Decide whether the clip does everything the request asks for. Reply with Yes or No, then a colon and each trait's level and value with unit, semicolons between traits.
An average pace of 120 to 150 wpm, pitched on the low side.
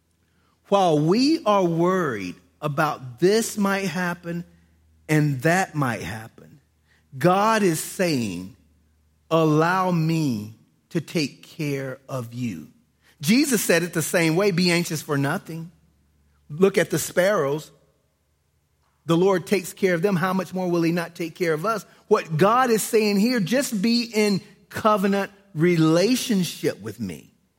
No: average, 140 wpm; medium, 170 Hz